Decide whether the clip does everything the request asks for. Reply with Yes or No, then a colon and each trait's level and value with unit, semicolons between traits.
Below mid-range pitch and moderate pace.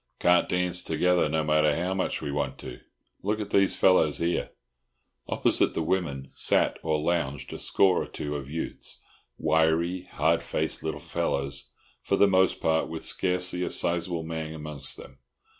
Yes: very low, 80 Hz; average, 160 wpm